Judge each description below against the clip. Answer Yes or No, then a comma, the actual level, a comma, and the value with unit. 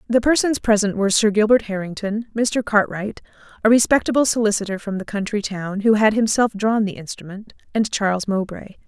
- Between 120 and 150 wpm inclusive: No, average, 170 wpm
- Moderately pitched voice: No, high, 210 Hz